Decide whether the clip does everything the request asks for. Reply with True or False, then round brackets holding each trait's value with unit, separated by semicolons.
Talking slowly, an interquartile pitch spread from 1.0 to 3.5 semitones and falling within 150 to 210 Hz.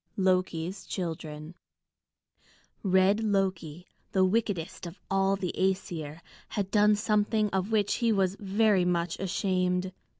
True (120 wpm; 2.4 semitones; 190 Hz)